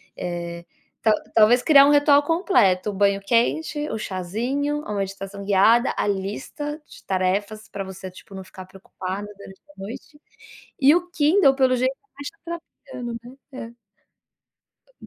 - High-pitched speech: Yes, high, 220 Hz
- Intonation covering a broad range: Yes, wide, 6.7 semitones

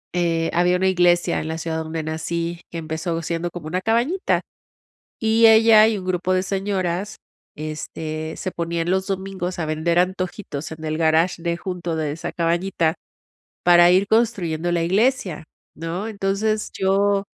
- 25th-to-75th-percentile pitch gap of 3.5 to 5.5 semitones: No, average, 2.9 semitones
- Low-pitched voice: No, medium, 175 Hz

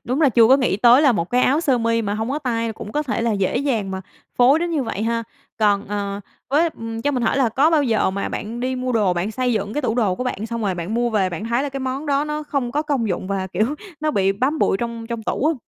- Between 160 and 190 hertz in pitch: No, high, 235 Hz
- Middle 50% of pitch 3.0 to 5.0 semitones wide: Yes, average, 4.5 semitones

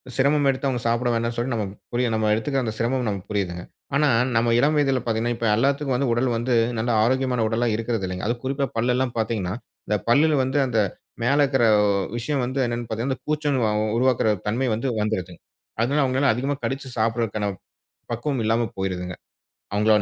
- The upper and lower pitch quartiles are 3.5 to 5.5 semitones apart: No, average, 3.1 semitones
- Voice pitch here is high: No, low, 120 Hz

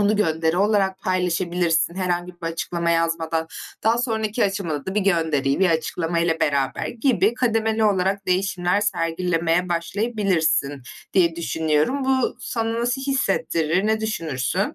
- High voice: No, medium, 180 Hz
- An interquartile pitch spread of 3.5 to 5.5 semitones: Yes, average, 4.3 semitones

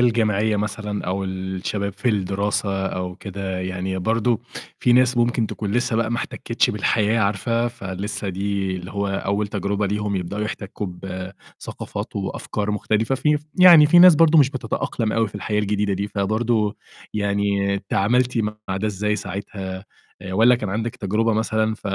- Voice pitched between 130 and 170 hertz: No, low, 105 Hz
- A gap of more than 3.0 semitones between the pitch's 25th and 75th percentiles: No, narrow, 2.5 semitones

